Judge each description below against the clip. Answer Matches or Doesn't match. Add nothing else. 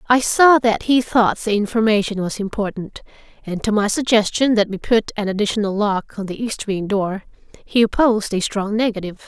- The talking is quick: Doesn't match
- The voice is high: Matches